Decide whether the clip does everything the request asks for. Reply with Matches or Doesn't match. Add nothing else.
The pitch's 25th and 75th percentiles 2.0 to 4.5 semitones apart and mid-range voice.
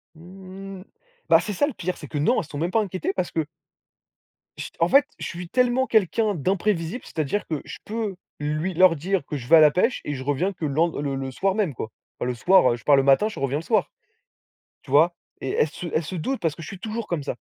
Doesn't match